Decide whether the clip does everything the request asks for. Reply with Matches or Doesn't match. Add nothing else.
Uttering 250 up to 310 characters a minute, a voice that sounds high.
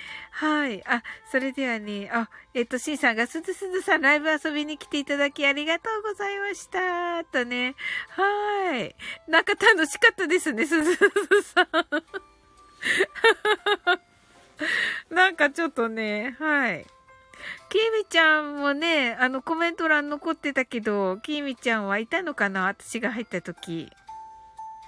Matches